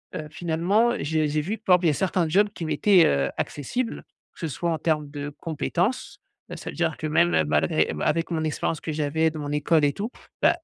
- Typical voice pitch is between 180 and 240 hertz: No, medium, 160 Hz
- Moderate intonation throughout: Yes, average, 3.1 semitones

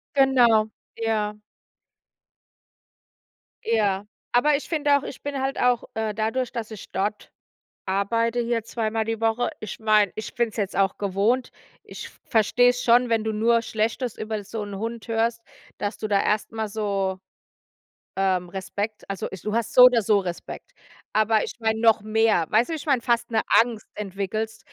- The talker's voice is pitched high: Yes, high, 220 Hz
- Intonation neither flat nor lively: No, narrow, 2.0 semitones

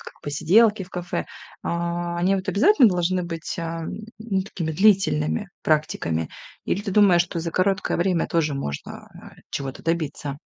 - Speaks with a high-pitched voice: No, medium, 175 Hz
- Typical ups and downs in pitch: Yes, average, 3.4 semitones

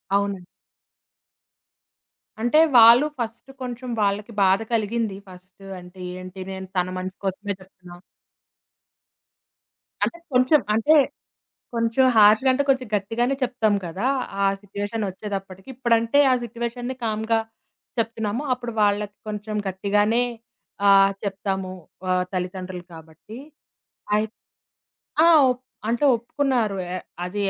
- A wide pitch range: No, average, 3.7 semitones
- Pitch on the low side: No, high, 210 Hz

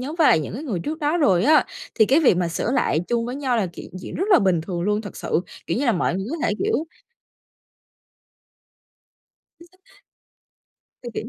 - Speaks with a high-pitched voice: Yes, high, 235 Hz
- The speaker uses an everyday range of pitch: No, wide, 8.3 semitones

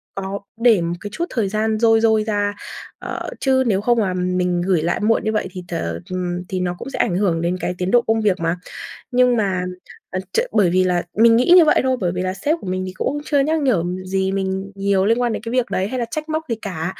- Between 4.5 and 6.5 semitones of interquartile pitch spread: No, average, 4.1 semitones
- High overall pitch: Yes, high, 200 Hz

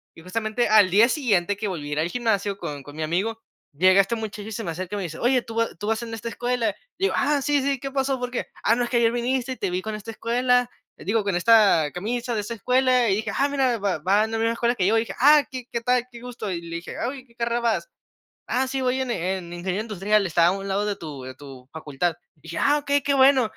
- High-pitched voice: Yes, high, 225 Hz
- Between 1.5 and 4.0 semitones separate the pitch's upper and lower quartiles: No, average, 4.8 semitones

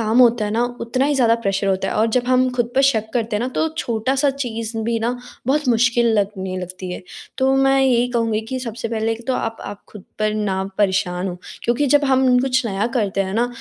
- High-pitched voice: Yes, high, 230 Hz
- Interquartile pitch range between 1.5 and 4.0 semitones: Yes, average, 3.3 semitones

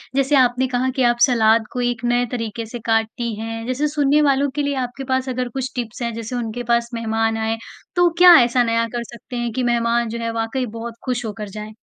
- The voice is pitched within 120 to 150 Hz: No, high, 235 Hz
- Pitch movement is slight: Yes, narrow, 2.1 semitones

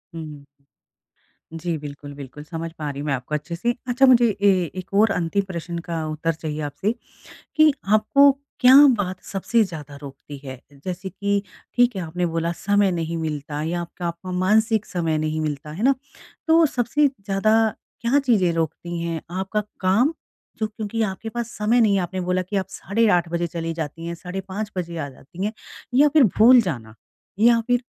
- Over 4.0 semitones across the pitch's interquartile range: Yes, average, 5.1 semitones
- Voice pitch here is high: No, medium, 180 Hz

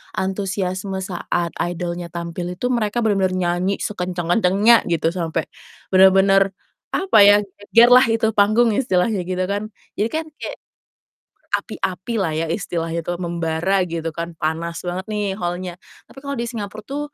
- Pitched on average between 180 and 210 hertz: Yes, medium, 185 Hz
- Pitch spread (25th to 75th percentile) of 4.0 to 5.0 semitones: No, average, 3.3 semitones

